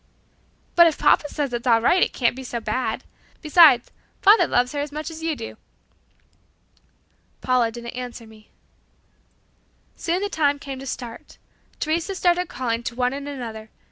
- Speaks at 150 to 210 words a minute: Yes, average, 170 wpm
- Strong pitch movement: No, average, 4.9 semitones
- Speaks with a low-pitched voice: No, very high, 265 Hz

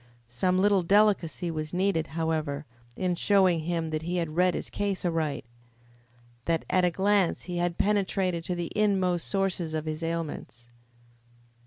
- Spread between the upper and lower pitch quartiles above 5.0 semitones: No, average, 2.8 semitones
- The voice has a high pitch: No, medium, 175 Hz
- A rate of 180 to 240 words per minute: No, average, 155 wpm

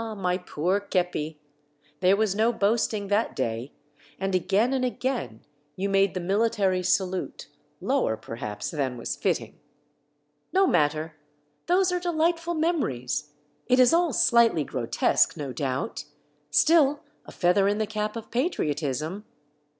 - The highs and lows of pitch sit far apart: Yes, wide, 7.9 semitones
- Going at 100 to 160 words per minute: Yes, average, 140 wpm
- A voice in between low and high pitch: No, high, 195 Hz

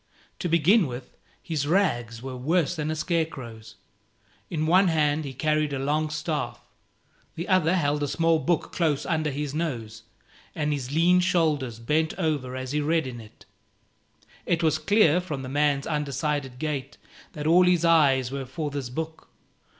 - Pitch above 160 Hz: No, medium, 150 Hz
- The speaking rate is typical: Yes, average, 165 wpm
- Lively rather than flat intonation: No, average, 3.3 semitones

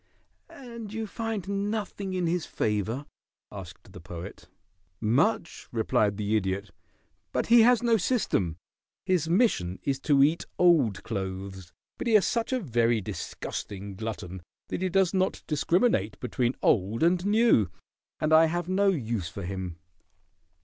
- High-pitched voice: No, medium, 145 Hz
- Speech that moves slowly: No, average, 145 wpm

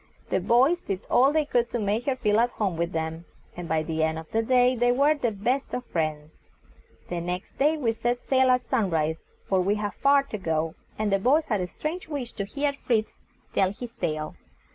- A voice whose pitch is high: Yes, high, 220 Hz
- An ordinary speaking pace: No, fast, 225 wpm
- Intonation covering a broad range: Yes, wide, 6.5 semitones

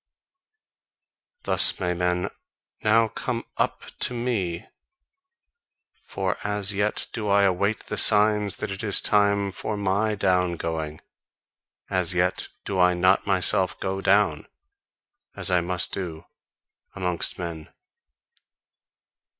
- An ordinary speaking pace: No, slow, 120 wpm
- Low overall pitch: Yes, very low, 95 Hz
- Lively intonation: No, narrow, 2.5 semitones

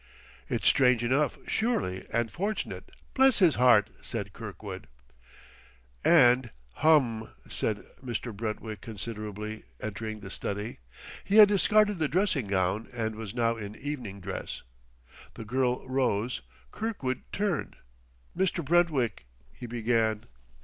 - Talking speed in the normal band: No, slow, 120 wpm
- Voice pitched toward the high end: No, low, 120 Hz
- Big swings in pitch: Yes, wide, 5.8 semitones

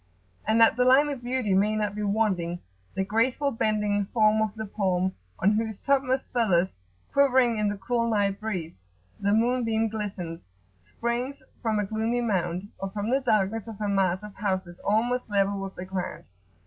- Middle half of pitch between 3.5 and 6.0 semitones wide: No, average, 3.1 semitones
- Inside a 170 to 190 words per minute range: Yes, average, 175 wpm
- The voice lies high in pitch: Yes, high, 215 Hz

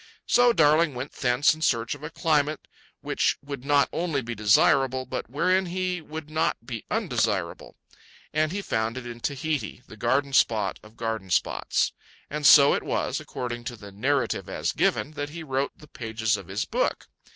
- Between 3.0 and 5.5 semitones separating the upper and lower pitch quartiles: Yes, average, 4.7 semitones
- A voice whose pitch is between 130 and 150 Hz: Yes, medium, 140 Hz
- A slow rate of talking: No, average, 180 wpm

